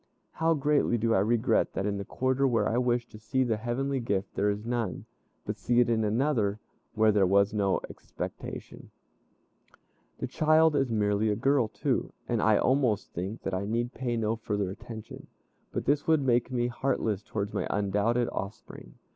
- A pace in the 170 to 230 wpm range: Yes, average, 180 wpm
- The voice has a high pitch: No, low, 115 Hz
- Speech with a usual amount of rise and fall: Yes, average, 3.7 semitones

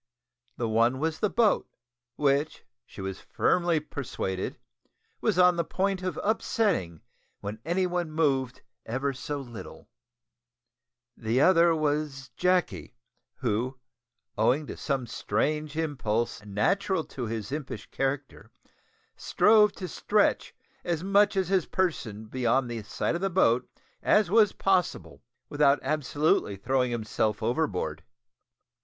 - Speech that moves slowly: Yes, slow, 125 wpm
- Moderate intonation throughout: No, wide, 6.9 semitones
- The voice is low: No, medium, 145 Hz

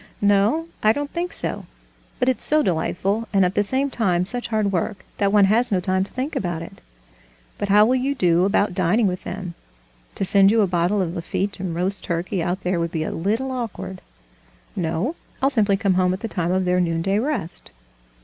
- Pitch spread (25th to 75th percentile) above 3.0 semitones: Yes, average, 3.8 semitones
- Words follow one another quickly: Yes, fast, 210 wpm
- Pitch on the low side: No, high, 195 Hz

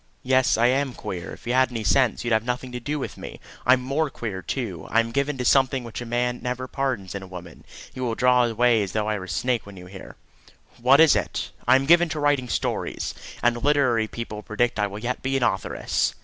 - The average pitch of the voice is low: Yes, low, 120 Hz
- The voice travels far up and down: No, average, 3.3 semitones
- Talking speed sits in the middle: No, fast, 240 wpm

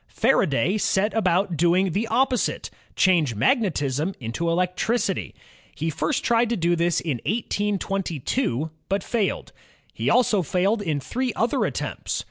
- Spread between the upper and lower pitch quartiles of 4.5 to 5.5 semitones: Yes, average, 5.2 semitones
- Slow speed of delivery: Yes, slow, 130 wpm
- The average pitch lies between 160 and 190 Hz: Yes, medium, 185 Hz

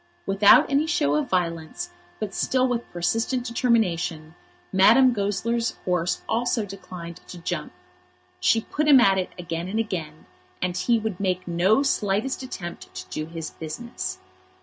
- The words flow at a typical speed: Yes, average, 150 wpm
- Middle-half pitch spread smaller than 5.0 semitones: No, wide, 5.4 semitones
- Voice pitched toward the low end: No, high, 195 Hz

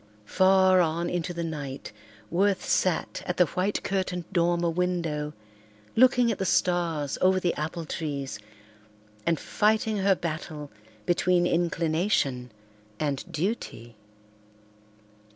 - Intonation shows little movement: No, average, 3.0 semitones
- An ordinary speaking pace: No, slow, 115 wpm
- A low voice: No, medium, 175 Hz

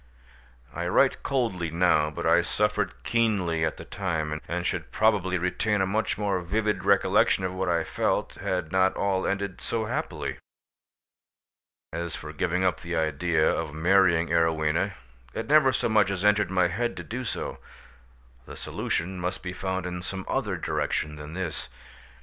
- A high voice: No, very low, 90 Hz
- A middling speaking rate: Yes, average, 165 wpm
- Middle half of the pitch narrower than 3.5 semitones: Yes, average, 3.1 semitones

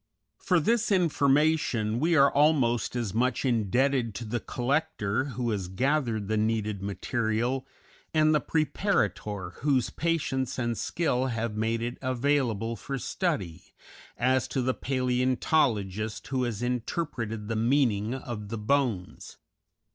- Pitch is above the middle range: No, low, 125 Hz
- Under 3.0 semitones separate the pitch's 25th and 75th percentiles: No, average, 4.1 semitones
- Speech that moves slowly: Yes, slow, 130 wpm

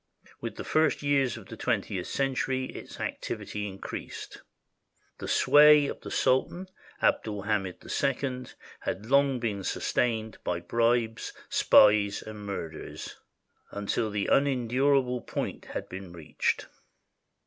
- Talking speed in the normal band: No, slow, 125 wpm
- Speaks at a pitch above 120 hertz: No, low, 115 Hz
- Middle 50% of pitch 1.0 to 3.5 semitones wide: No, average, 4.8 semitones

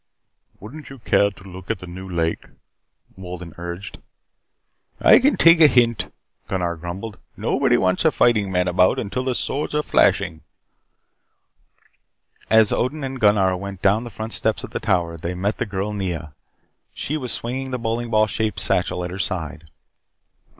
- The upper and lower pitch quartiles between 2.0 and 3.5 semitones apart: No, average, 4.7 semitones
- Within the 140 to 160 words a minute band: No, average, 170 wpm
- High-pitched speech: No, low, 100 Hz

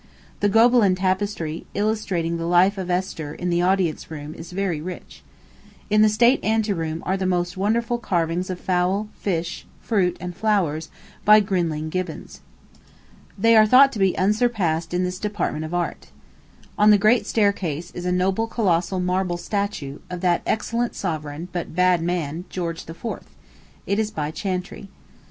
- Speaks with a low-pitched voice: No, medium, 185 Hz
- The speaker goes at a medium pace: Yes, average, 160 wpm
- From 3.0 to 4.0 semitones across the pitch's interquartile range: Yes, average, 3.4 semitones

